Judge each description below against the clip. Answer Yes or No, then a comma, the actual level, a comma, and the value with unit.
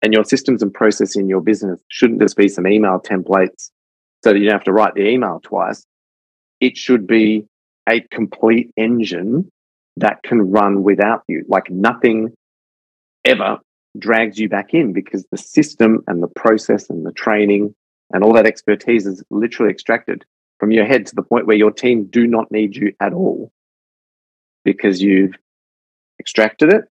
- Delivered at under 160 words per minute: No, average, 170 wpm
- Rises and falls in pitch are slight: Yes, narrow, 2.2 semitones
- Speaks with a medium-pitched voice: No, low, 105 Hz